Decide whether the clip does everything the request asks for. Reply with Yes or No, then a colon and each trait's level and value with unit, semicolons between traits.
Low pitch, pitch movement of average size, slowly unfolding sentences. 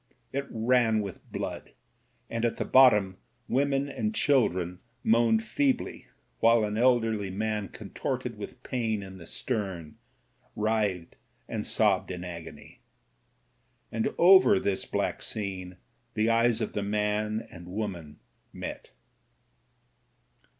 Yes: low, 110 Hz; average, 3.7 semitones; slow, 125 wpm